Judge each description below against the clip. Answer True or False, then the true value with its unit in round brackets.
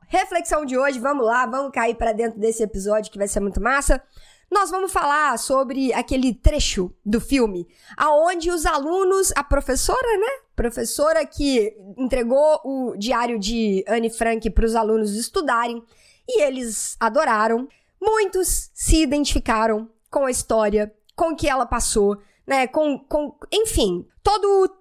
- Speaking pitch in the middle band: False (260 Hz)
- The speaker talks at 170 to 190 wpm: False (150 wpm)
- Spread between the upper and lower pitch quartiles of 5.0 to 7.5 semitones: True (5.4 semitones)